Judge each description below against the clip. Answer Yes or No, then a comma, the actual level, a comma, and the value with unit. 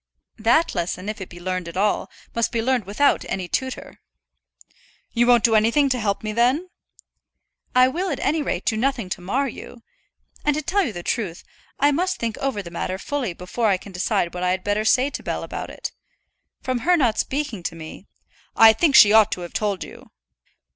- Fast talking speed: Yes, fast, 210 wpm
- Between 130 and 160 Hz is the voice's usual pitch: No, high, 225 Hz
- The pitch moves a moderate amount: No, wide, 6.1 semitones